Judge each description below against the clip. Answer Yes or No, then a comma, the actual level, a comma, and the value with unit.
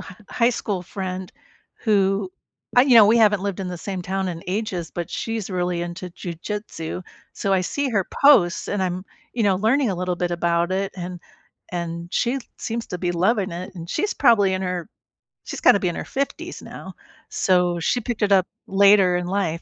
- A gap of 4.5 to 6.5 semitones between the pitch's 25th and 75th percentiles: No, average, 2.8 semitones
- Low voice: No, high, 190 Hz